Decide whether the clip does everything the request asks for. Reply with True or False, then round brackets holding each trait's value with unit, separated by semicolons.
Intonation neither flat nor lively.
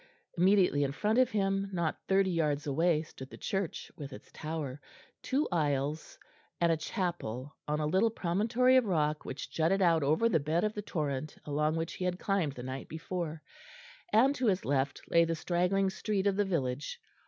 True (4.5 semitones)